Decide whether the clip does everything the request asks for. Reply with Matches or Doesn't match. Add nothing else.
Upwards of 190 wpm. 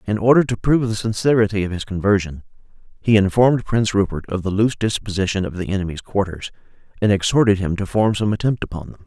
Matches